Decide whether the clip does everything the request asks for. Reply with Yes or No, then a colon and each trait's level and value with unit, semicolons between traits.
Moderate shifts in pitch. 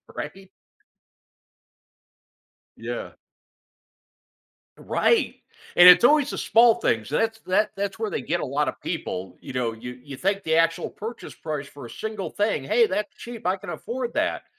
No: wide, 7.4 semitones